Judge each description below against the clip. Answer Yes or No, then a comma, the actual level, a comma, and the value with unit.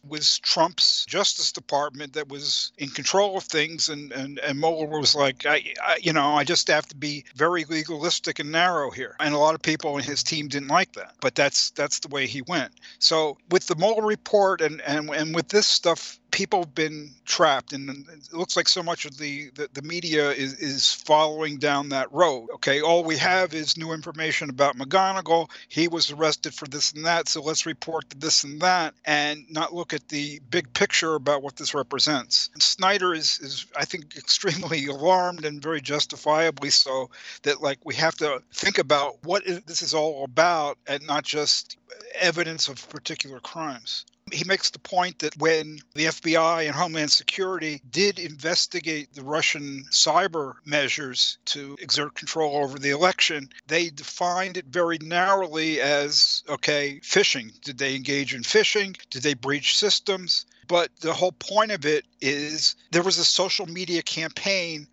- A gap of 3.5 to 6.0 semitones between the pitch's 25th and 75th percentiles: No, average, 3.1 semitones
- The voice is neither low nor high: Yes, medium, 155 Hz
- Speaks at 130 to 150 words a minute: No, average, 185 wpm